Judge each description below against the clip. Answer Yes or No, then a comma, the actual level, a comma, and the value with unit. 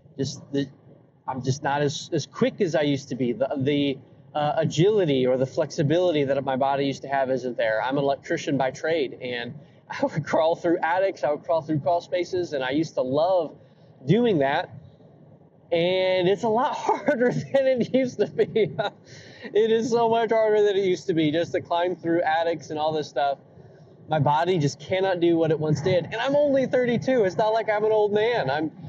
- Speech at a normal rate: No, fast, 210 wpm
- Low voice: No, medium, 160 Hz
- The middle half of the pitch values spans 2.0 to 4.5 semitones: No, wide, 5.6 semitones